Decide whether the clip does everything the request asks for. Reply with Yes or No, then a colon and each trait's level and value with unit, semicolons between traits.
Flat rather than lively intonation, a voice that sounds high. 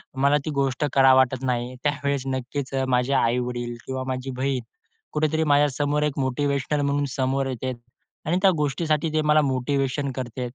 No: narrow, 2.1 semitones; low, 135 Hz